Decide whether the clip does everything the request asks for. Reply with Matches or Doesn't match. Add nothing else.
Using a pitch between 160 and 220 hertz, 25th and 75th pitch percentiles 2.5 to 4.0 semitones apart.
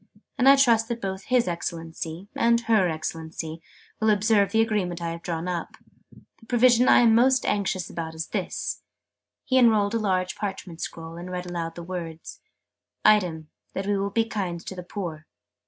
Doesn't match